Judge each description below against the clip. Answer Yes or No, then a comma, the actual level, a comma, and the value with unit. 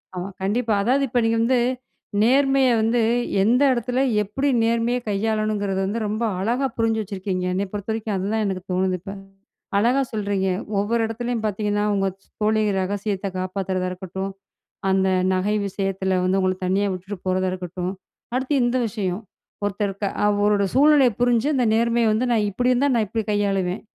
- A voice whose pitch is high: Yes, high, 210 Hz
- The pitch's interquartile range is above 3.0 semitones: Yes, average, 3.4 semitones